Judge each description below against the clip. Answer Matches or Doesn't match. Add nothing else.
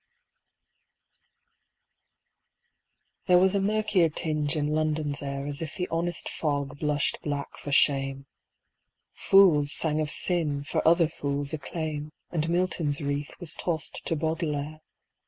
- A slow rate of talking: Matches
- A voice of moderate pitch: Matches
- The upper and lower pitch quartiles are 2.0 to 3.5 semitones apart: Matches